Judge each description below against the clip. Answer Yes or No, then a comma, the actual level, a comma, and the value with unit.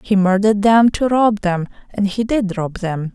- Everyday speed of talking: No, fast, 210 wpm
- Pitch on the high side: Yes, high, 200 Hz